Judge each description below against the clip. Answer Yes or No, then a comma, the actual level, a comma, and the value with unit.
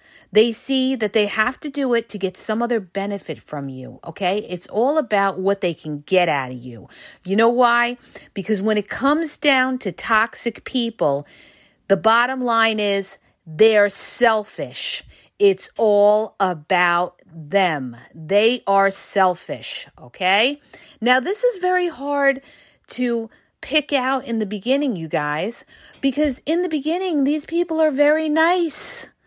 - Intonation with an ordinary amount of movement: No, wide, 6.3 semitones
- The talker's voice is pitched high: Yes, high, 220 Hz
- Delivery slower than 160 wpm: Yes, average, 150 wpm